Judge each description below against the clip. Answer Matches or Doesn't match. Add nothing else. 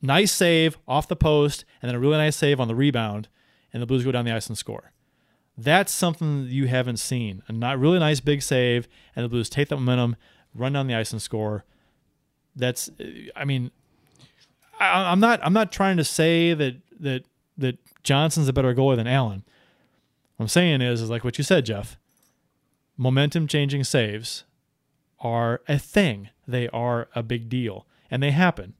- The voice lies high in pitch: Doesn't match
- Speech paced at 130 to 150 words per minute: Doesn't match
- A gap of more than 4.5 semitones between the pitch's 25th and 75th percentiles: Doesn't match